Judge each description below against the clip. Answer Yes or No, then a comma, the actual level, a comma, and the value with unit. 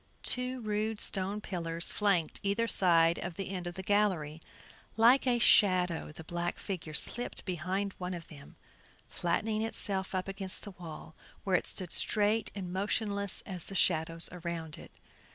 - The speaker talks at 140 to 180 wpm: Yes, average, 160 wpm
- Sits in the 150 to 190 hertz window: Yes, medium, 185 Hz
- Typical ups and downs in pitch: Yes, average, 3.3 semitones